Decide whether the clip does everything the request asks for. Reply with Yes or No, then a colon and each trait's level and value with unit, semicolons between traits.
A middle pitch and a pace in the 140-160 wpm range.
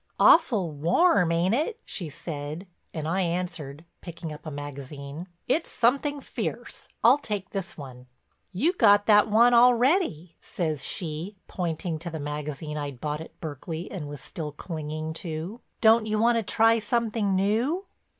Yes: medium, 175 Hz; average, 150 wpm